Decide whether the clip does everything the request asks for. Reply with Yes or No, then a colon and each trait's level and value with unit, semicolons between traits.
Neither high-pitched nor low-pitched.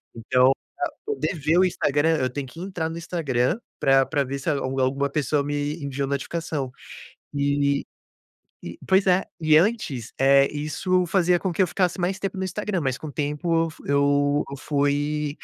Yes: medium, 150 Hz